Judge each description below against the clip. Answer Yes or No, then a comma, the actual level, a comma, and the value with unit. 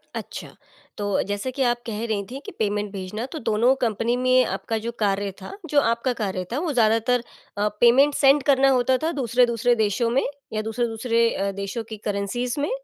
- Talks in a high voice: Yes, high, 235 Hz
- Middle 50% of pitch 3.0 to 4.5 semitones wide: Yes, average, 3.4 semitones